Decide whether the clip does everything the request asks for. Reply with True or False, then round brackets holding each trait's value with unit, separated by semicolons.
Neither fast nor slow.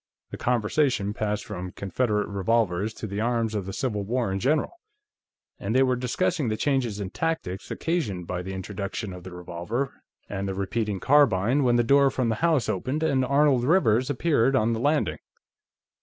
True (180 wpm)